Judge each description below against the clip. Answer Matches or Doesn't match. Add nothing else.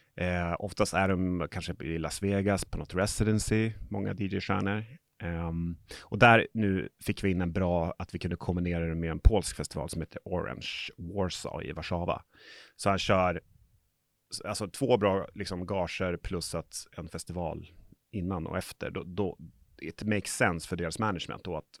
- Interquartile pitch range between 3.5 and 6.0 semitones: Doesn't match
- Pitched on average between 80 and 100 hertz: Matches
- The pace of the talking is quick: Doesn't match